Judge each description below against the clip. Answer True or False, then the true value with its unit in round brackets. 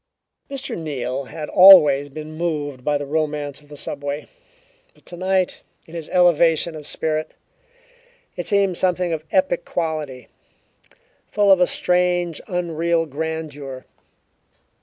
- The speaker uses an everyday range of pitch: True (3.4 semitones)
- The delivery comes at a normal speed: False (125 wpm)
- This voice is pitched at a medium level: True (160 Hz)